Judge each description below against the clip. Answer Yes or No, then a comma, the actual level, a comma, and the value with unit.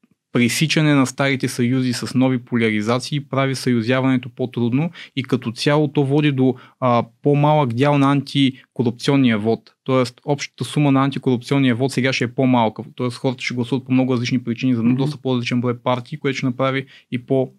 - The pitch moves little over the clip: Yes, narrow, 2.0 semitones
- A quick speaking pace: Yes, fast, 175 wpm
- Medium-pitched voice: No, low, 130 Hz